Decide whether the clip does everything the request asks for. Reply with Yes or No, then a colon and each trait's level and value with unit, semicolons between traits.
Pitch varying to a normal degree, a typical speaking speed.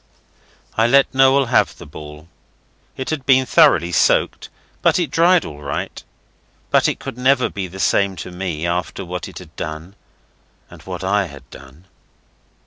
No: wide, 8.7 semitones; average, 165 wpm